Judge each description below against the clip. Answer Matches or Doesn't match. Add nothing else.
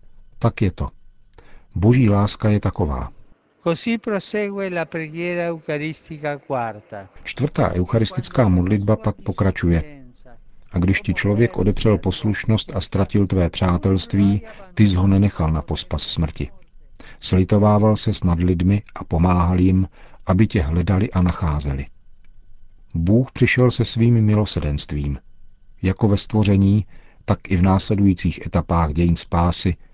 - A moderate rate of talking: Doesn't match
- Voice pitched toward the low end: Matches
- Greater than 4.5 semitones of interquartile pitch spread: Doesn't match